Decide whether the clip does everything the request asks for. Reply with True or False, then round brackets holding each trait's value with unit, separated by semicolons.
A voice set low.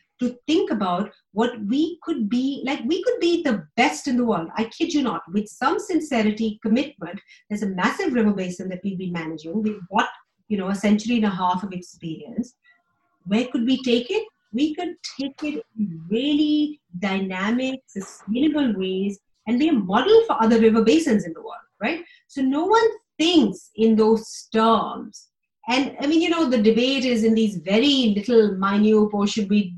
False (225 Hz)